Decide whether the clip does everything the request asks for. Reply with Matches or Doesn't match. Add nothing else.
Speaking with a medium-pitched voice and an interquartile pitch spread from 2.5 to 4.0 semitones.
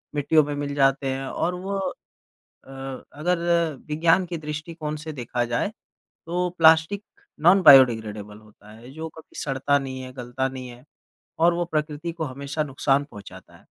Matches